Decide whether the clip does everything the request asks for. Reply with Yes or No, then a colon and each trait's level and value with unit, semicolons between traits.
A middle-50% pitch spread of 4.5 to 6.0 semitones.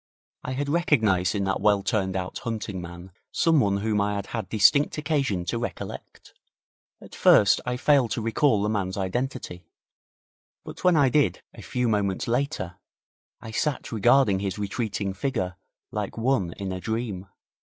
Yes: average, 5.0 semitones